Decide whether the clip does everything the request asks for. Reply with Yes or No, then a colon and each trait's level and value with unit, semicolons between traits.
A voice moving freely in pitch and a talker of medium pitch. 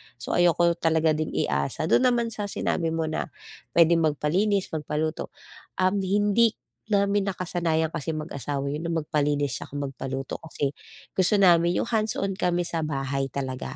No: average, 4.4 semitones; medium, 165 Hz